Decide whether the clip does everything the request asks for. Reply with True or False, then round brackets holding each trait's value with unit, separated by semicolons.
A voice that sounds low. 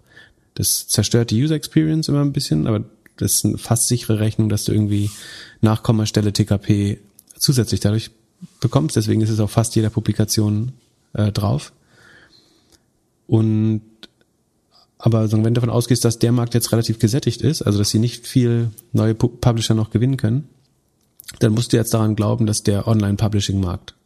True (110 Hz)